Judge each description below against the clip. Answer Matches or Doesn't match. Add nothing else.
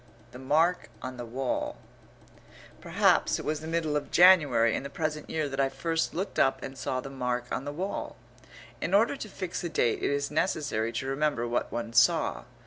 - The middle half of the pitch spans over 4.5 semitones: Doesn't match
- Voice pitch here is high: Doesn't match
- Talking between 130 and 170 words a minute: Doesn't match